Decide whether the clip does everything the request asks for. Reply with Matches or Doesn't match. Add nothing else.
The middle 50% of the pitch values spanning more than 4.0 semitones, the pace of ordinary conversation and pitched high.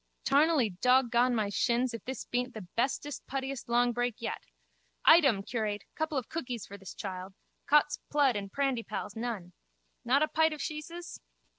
Matches